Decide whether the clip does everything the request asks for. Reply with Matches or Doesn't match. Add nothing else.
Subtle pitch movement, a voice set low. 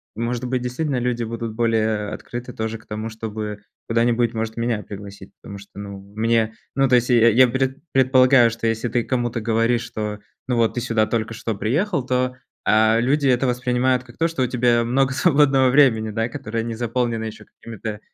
Matches